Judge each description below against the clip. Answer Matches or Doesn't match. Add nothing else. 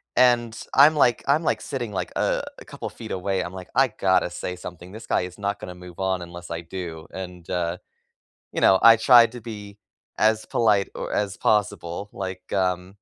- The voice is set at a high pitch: Doesn't match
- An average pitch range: Matches